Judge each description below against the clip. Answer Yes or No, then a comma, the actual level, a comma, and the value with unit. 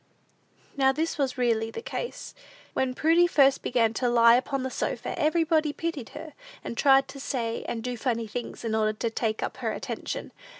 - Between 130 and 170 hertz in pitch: No, very high, 255 Hz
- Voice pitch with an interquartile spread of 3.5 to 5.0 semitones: Yes, average, 4.1 semitones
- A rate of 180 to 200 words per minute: Yes, average, 185 wpm